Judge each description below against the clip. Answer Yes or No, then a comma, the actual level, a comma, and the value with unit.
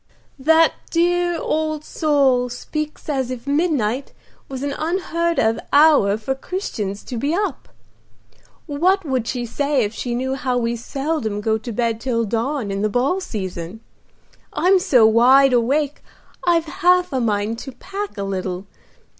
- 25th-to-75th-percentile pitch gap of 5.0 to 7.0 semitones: Yes, wide, 5.4 semitones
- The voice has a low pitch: No, very high, 265 Hz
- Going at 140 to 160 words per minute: Yes, average, 155 wpm